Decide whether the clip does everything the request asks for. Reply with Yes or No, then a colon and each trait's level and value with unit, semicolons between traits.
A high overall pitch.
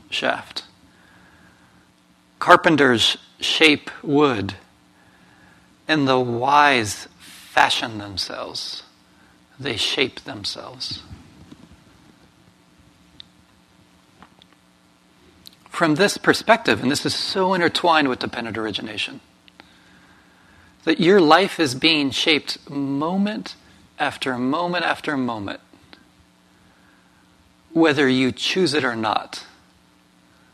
No: low, 100 Hz